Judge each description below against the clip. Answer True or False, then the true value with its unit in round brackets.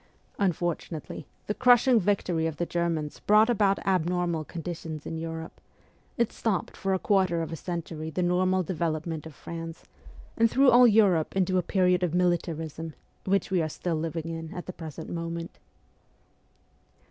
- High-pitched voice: False (175 Hz)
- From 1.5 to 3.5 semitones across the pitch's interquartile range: True (2.7 semitones)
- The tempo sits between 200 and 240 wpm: False (160 wpm)